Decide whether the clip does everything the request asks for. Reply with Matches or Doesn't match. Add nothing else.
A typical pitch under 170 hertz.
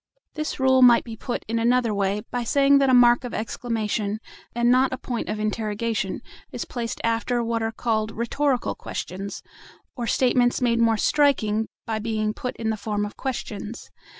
Doesn't match